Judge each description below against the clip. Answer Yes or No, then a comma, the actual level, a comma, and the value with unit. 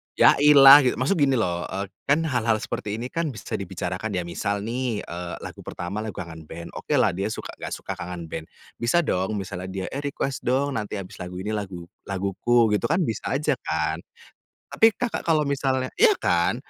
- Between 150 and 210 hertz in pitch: No, low, 110 Hz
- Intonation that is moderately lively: No, wide, 6.8 semitones